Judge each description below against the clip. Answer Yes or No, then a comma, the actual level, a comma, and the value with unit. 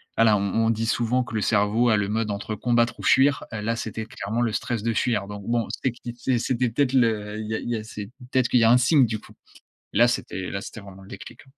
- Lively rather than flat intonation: No, narrow, 2.4 semitones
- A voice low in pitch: Yes, low, 115 Hz